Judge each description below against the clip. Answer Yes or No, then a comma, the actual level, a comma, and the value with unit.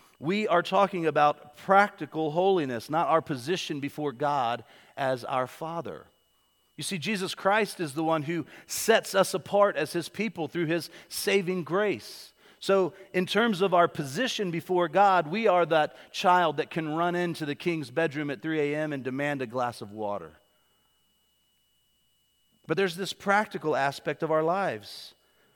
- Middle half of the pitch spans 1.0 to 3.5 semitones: No, average, 4.4 semitones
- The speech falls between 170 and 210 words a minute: No, average, 160 wpm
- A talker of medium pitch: Yes, medium, 165 Hz